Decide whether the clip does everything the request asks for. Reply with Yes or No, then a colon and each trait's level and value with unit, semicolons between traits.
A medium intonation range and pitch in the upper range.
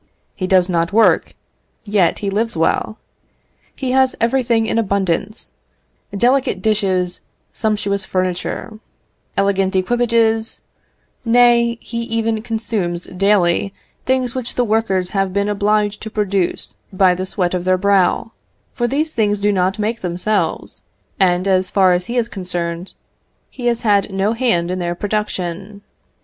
Yes: average, 3.5 semitones; high, 200 Hz